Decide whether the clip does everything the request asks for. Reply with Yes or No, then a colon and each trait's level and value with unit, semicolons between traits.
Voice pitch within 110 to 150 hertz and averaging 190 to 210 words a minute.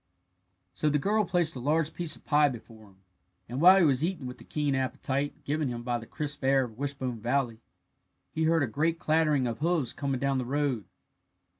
Yes: medium, 140 Hz; fast, 205 wpm